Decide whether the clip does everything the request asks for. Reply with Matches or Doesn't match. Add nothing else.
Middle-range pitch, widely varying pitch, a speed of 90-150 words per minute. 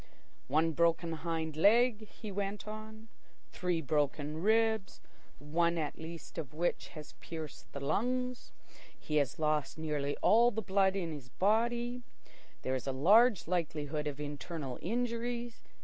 Matches